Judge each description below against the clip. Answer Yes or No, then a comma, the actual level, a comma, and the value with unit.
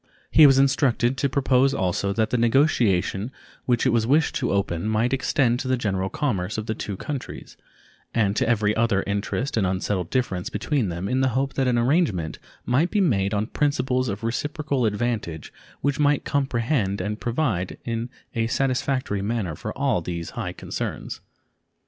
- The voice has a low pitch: Yes, low, 115 Hz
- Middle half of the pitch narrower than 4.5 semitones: No, average, 5.0 semitones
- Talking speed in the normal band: Yes, average, 175 wpm